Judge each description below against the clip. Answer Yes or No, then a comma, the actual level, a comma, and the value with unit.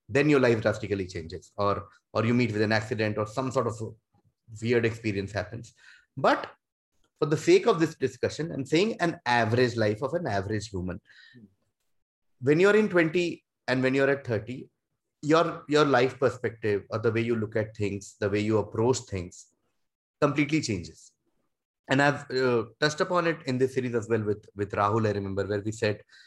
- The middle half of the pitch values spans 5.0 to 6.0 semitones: Yes, wide, 5.4 semitones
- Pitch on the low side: Yes, low, 115 Hz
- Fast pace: No, average, 190 wpm